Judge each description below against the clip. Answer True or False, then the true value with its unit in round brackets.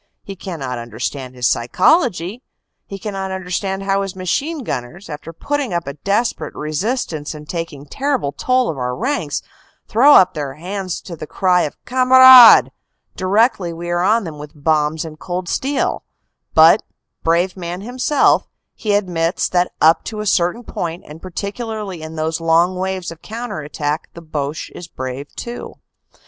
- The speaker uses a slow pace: False (160 wpm)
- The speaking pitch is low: False (180 Hz)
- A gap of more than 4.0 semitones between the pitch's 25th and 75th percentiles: True (5.1 semitones)